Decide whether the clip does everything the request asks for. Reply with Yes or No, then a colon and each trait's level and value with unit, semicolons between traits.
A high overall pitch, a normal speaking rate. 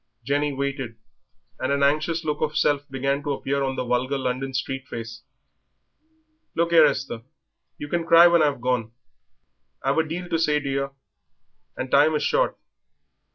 No: medium, 140 Hz; average, 165 wpm